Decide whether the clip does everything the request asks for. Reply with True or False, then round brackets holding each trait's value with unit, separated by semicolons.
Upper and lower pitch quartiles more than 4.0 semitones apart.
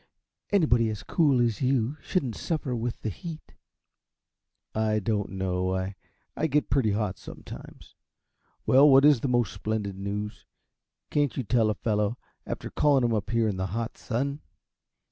True (4.6 semitones)